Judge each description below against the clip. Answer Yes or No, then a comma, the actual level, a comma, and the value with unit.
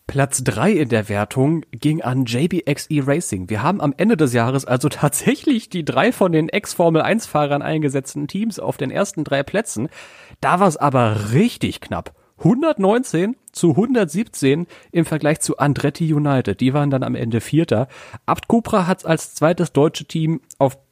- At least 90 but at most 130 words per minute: No, average, 165 wpm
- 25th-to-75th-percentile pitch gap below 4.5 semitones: No, average, 4.9 semitones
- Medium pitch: Yes, medium, 155 Hz